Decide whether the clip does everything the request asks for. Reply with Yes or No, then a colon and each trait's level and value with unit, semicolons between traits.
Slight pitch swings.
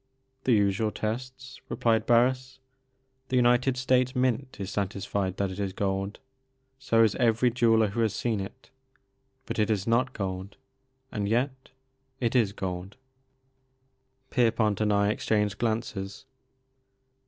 No: average, 3.9 semitones